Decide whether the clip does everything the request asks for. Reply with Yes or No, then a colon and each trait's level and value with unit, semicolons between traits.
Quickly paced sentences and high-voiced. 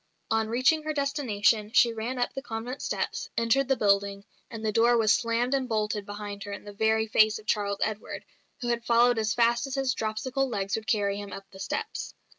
Yes: fast, 215 wpm; high, 225 Hz